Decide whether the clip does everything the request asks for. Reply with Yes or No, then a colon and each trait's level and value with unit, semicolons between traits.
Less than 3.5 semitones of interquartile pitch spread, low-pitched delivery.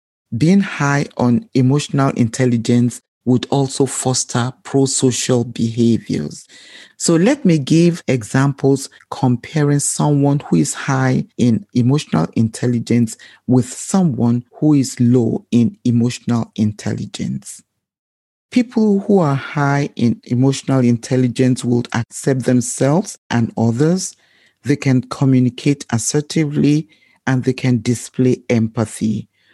Yes: average, 3.1 semitones; low, 130 Hz